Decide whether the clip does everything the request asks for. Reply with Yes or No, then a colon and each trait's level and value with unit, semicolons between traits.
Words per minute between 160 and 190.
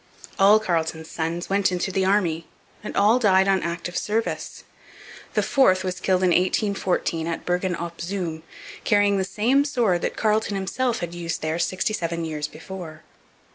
Yes: average, 165 wpm